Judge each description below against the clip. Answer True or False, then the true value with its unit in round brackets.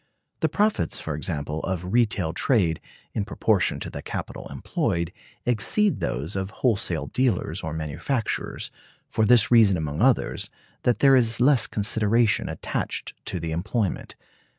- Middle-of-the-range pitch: False (100 Hz)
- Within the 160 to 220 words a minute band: False (140 wpm)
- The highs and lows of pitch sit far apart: True (6.3 semitones)